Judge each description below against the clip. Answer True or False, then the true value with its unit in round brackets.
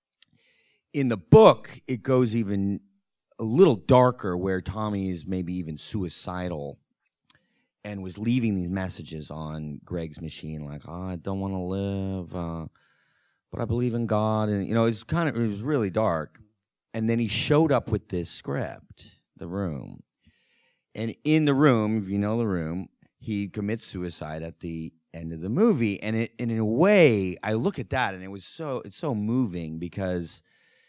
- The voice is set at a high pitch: False (100 Hz)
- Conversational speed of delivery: True (180 wpm)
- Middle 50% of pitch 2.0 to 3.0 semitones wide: False (4.4 semitones)